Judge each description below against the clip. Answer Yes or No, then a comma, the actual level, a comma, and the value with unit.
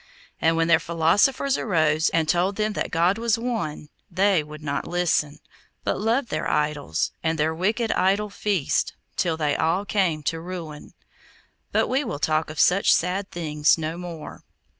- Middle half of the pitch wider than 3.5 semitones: Yes, average, 4.4 semitones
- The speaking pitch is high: No, medium, 170 Hz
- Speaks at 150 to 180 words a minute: Yes, average, 165 wpm